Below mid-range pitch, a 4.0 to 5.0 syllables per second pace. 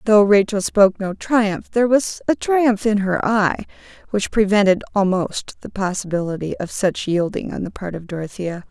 No: high, 200 Hz; 4.9 syllables/s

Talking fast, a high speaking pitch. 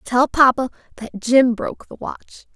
No: average, 165 wpm; very high, 250 Hz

